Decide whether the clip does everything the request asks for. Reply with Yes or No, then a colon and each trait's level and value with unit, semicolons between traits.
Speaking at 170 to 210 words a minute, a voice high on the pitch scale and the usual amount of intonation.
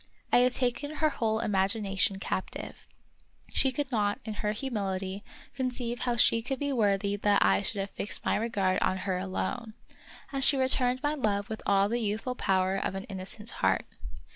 Yes: average, 180 wpm; high, 215 Hz; average, 4.3 semitones